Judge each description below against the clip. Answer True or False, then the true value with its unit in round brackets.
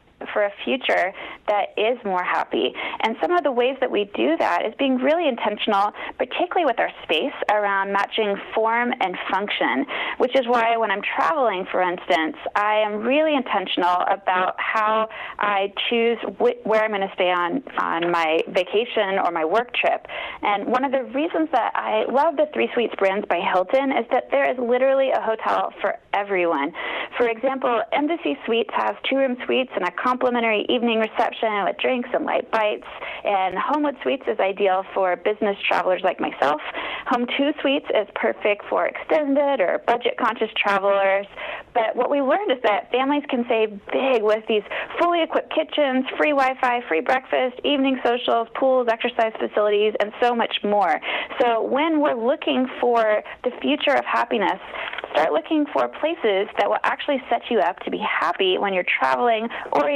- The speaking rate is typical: True (175 wpm)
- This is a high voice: True (235 Hz)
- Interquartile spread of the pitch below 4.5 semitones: False (5.0 semitones)